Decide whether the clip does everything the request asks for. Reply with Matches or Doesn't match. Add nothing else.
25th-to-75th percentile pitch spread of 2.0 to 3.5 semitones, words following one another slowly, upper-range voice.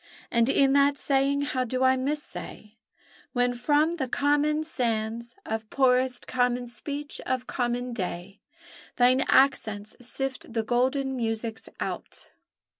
Matches